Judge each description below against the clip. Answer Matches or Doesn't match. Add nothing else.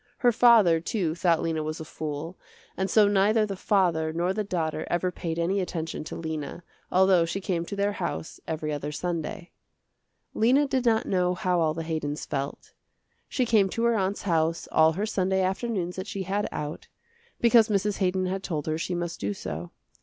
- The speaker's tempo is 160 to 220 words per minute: Matches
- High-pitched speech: Doesn't match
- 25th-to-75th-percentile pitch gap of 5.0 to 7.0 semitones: Doesn't match